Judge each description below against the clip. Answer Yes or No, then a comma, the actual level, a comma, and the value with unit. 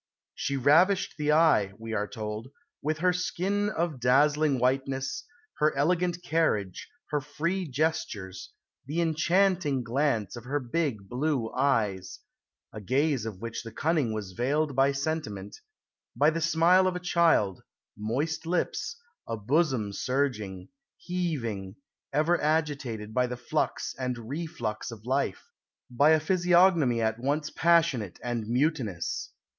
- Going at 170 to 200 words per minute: No, slow, 135 wpm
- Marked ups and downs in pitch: Yes, wide, 6.0 semitones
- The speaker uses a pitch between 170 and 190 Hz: No, medium, 140 Hz